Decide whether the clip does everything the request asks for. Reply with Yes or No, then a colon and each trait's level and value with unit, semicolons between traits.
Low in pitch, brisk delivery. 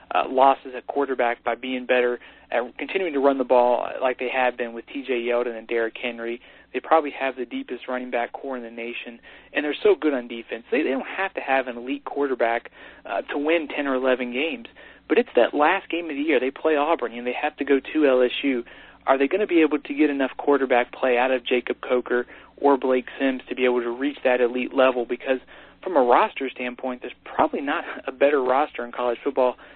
Yes: low, 130 Hz; fast, 230 wpm